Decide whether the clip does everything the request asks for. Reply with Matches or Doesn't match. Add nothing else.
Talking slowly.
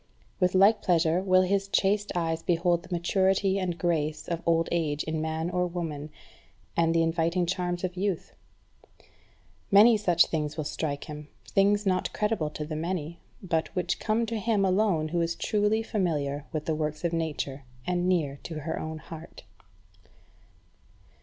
Doesn't match